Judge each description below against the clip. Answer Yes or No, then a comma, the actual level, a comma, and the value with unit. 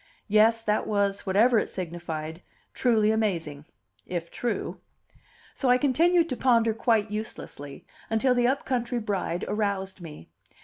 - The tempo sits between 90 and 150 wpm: Yes, slow, 135 wpm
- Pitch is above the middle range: Yes, high, 215 Hz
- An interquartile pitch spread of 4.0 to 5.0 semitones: Yes, average, 4.7 semitones